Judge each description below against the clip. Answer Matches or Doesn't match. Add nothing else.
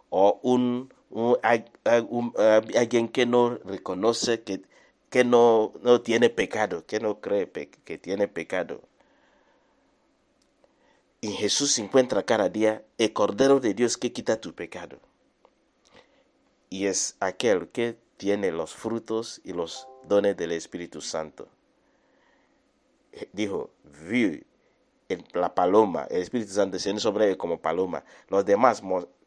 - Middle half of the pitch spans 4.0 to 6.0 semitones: Doesn't match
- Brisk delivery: Doesn't match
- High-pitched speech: Doesn't match